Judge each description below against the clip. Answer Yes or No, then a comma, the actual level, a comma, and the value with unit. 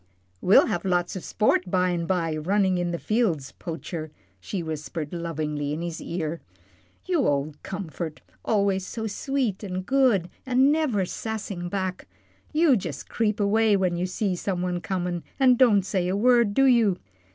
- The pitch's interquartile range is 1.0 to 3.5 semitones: No, average, 4.2 semitones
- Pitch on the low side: No, medium, 185 Hz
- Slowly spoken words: No, average, 165 wpm